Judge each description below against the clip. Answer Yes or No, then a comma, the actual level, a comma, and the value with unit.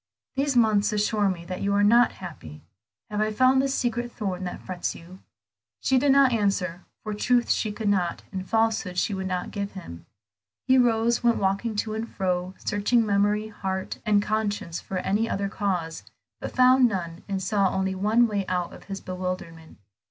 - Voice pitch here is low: No, high, 205 Hz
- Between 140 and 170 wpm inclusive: No, average, 185 wpm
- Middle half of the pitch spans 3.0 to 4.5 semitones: Yes, average, 3.4 semitones